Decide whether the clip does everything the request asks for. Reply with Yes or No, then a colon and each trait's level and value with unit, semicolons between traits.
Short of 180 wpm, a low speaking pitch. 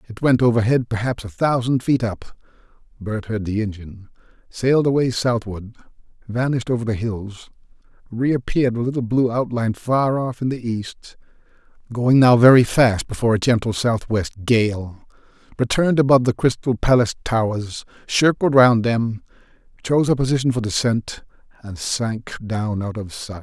Yes: average, 150 wpm; low, 115 Hz